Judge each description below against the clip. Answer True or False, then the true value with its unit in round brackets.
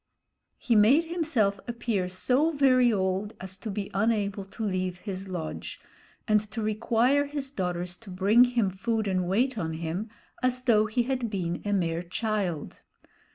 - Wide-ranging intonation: False (4.4 semitones)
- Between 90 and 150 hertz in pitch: False (210 Hz)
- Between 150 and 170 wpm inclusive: True (160 wpm)